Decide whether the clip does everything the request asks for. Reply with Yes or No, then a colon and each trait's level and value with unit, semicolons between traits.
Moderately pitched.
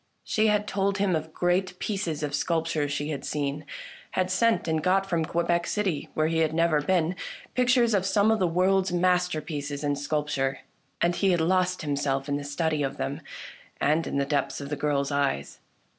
Yes: medium, 165 Hz